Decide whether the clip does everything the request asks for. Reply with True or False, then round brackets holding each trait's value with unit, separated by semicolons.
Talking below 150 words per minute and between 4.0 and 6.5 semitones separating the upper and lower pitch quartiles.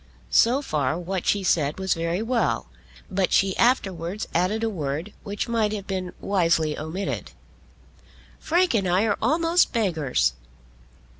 True (140 wpm; 4.8 semitones)